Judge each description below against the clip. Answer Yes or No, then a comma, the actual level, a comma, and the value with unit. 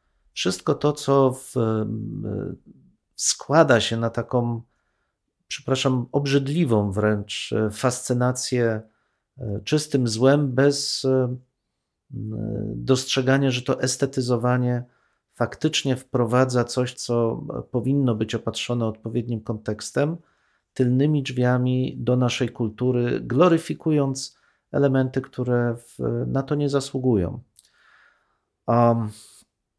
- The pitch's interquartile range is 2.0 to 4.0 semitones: Yes, average, 2.7 semitones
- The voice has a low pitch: Yes, low, 125 Hz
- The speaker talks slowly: Yes, slow, 85 wpm